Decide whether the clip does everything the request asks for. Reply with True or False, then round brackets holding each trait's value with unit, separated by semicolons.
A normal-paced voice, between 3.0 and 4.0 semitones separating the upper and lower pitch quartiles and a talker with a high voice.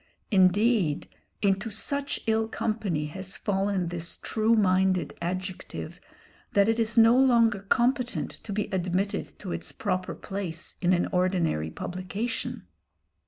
False (125 wpm; 3.4 semitones; 195 Hz)